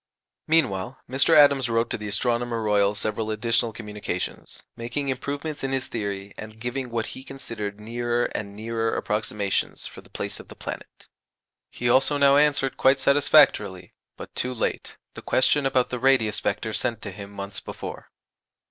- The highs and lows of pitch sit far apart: No, average, 4.1 semitones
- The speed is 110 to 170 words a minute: Yes, average, 165 wpm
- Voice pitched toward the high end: No, low, 115 Hz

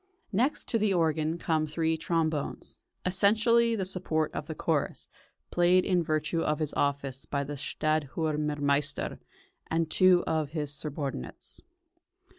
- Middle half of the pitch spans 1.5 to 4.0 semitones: Yes, average, 3.0 semitones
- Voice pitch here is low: No, medium, 160 Hz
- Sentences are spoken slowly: Yes, slow, 130 wpm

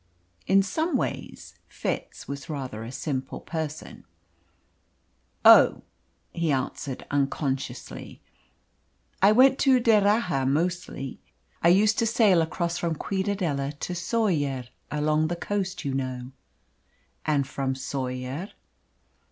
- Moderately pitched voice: Yes, medium, 160 Hz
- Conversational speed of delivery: No, slow, 110 wpm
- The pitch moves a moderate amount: No, wide, 6.2 semitones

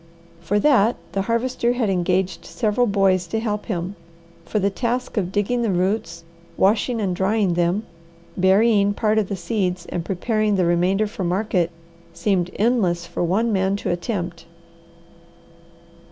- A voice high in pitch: Yes, high, 200 Hz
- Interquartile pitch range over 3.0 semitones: Yes, average, 3.4 semitones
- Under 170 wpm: Yes, average, 150 wpm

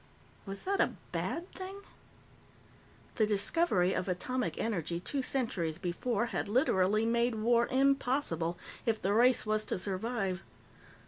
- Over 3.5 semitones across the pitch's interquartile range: Yes, average, 5.1 semitones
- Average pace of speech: No, slow, 130 wpm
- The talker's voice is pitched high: Yes, high, 225 Hz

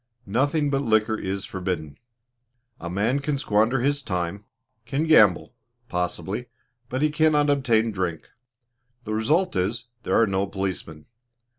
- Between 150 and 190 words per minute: No, slow, 135 wpm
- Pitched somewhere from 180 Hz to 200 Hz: No, low, 110 Hz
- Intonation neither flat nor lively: No, wide, 6.5 semitones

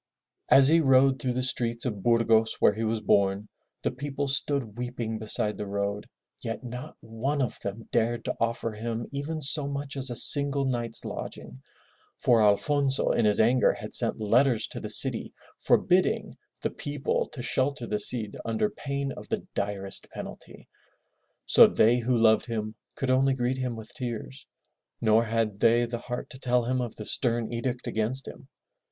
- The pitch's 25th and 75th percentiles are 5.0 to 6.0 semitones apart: No, average, 3.2 semitones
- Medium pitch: No, low, 120 Hz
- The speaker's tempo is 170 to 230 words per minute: Yes, average, 175 wpm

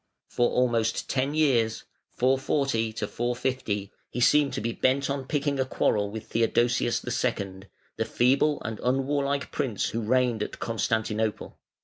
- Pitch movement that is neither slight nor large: Yes, average, 3.4 semitones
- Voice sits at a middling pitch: No, low, 120 Hz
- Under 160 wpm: Yes, slow, 135 wpm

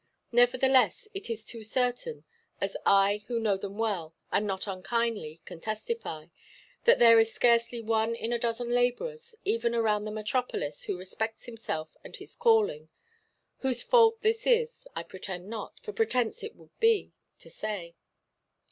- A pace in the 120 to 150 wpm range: Yes, average, 145 wpm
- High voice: Yes, high, 230 Hz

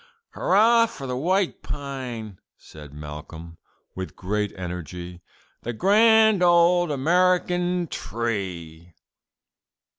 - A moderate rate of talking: No, slow, 95 wpm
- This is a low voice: Yes, low, 130 Hz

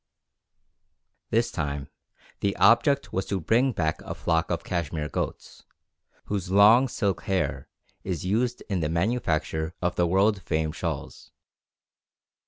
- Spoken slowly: Yes, slow, 130 wpm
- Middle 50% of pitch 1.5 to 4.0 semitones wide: No, average, 5.3 semitones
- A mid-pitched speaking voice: No, very low, 95 Hz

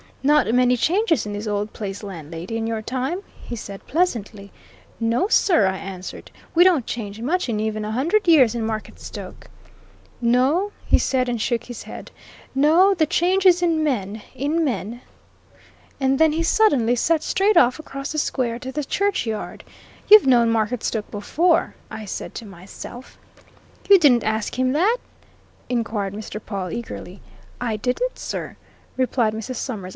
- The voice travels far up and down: Yes, wide, 6.5 semitones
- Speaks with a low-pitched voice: No, high, 245 Hz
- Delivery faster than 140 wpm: Yes, average, 160 wpm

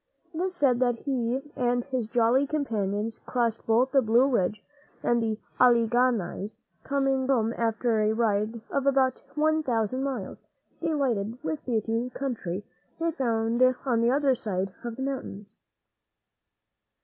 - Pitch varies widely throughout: No, average, 3.2 semitones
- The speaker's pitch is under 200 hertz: No, high, 240 Hz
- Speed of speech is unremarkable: Yes, average, 155 wpm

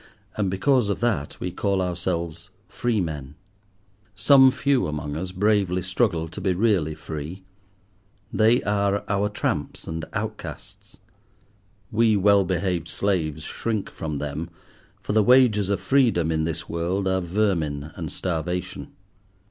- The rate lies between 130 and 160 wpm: Yes, slow, 135 wpm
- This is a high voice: No, very low, 95 Hz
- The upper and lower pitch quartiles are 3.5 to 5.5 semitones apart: Yes, average, 4.2 semitones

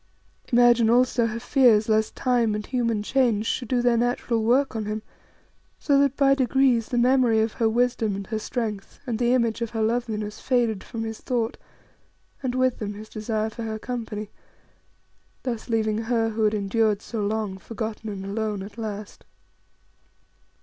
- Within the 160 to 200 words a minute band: Yes, average, 170 wpm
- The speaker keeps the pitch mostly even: Yes, narrow, 2.2 semitones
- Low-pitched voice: No, high, 225 Hz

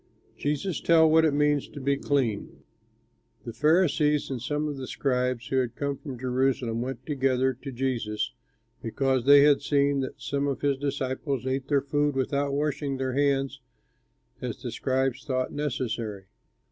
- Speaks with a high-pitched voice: No, low, 135 Hz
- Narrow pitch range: Yes, narrow, 1.9 semitones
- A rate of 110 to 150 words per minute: No, average, 160 wpm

